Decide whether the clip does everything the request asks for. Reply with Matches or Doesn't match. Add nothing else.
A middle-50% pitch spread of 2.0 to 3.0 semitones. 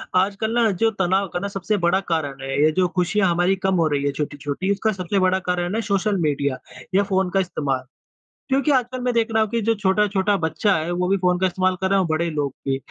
Doesn't match